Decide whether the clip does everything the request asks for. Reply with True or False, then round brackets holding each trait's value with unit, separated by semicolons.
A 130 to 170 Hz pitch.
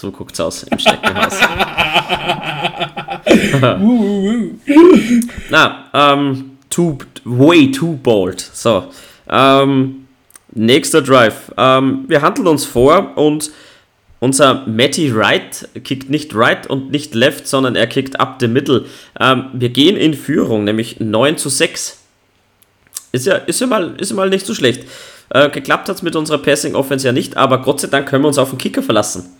True (135 Hz)